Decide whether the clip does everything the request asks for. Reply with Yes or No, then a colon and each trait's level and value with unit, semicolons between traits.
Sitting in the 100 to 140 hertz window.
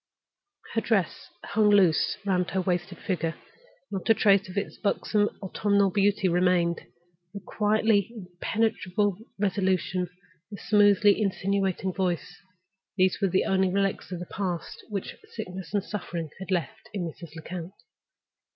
No: high, 190 Hz